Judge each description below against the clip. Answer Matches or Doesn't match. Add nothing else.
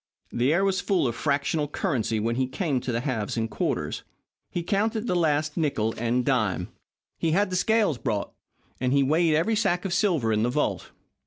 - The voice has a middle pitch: Matches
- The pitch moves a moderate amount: Doesn't match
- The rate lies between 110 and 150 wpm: Doesn't match